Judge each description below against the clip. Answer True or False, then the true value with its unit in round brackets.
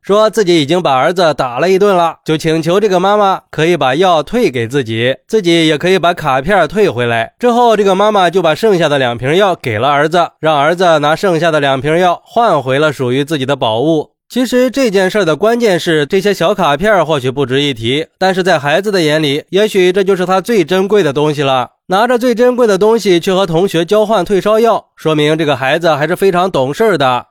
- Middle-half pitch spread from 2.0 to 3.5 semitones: False (5.4 semitones)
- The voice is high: False (175 Hz)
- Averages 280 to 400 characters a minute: True (325 characters per minute)